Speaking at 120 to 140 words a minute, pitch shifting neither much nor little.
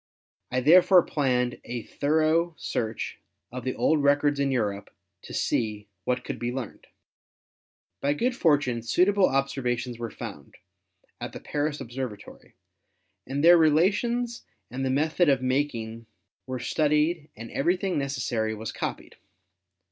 Yes: slow, 135 wpm; average, 4.5 semitones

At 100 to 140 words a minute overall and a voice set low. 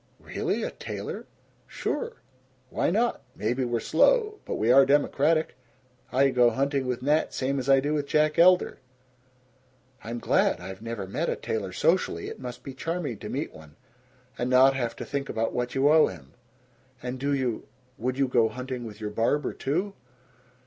No: average, 175 wpm; low, 130 Hz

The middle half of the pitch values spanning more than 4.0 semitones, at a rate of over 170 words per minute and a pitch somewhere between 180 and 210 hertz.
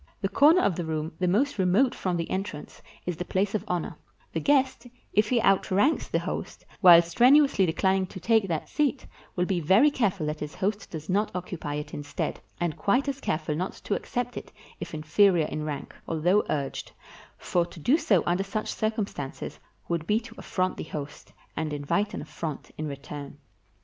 Yes: average, 5.3 semitones; average, 190 wpm; medium, 185 Hz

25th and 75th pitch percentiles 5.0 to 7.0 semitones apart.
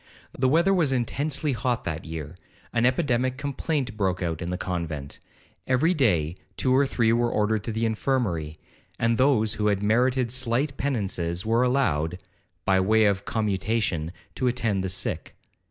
Yes: wide, 5.5 semitones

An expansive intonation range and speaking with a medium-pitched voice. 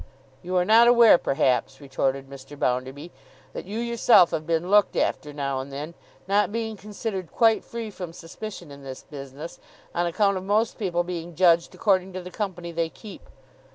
Yes: wide, 5.9 semitones; medium, 175 Hz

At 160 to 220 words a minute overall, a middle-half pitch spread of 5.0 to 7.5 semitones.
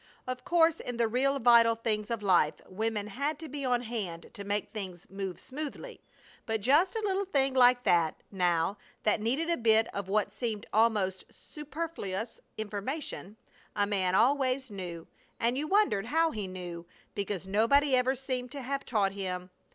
Yes: average, 170 wpm; wide, 5.4 semitones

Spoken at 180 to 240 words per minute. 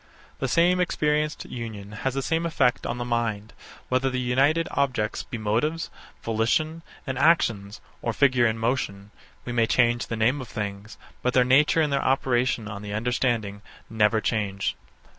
No: average, 165 wpm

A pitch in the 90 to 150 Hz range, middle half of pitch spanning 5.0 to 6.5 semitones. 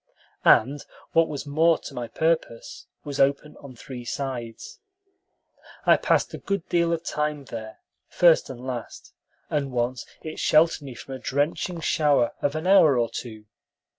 No: medium, 140 Hz; average, 4.3 semitones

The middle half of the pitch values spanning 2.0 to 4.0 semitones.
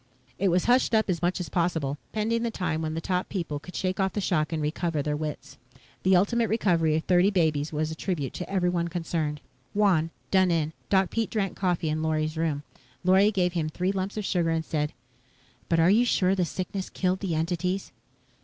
Yes: average, 3.3 semitones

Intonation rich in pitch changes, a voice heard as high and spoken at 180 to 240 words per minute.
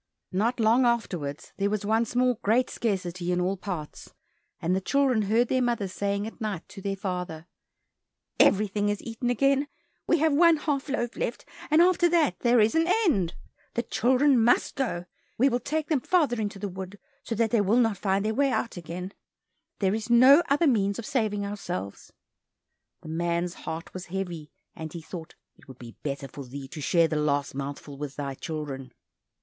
Yes: wide, 6.1 semitones; high, 205 Hz; average, 190 wpm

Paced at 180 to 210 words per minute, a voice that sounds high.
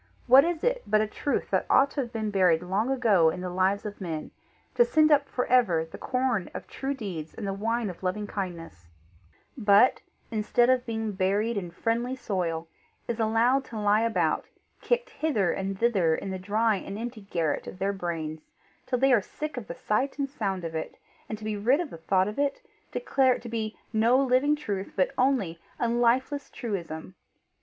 Yes: average, 200 wpm; high, 215 Hz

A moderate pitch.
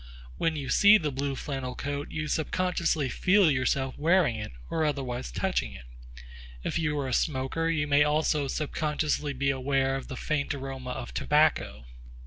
Yes: medium, 145 Hz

